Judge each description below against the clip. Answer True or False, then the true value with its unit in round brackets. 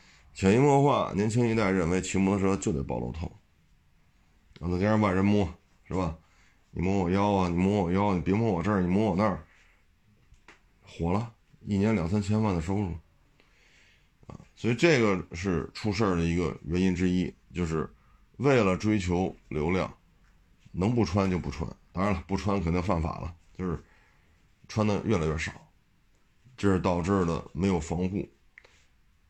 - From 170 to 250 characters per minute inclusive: True (245 characters per minute)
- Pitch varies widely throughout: False (3.5 semitones)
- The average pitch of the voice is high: False (95 Hz)